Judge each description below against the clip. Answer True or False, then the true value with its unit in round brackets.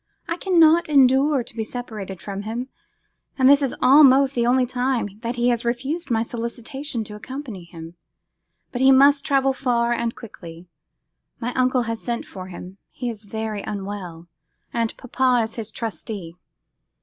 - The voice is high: True (235 Hz)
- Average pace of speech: True (160 wpm)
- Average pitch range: True (3.7 semitones)